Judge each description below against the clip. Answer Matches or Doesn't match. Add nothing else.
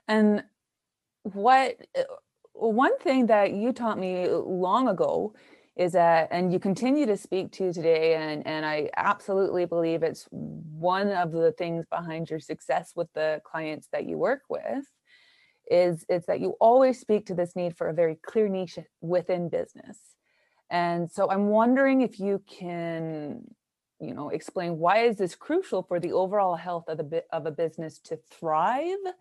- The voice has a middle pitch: Matches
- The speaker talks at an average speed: Matches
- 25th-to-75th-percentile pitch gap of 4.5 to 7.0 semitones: Matches